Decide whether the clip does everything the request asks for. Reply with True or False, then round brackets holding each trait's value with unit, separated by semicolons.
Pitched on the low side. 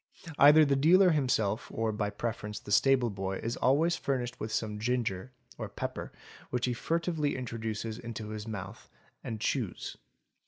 True (115 Hz)